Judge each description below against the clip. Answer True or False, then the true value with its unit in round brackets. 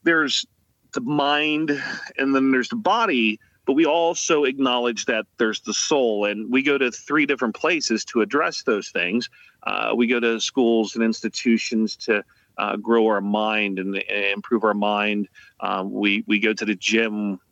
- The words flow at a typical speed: True (175 wpm)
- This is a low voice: True (110 Hz)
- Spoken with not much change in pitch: False (3.1 semitones)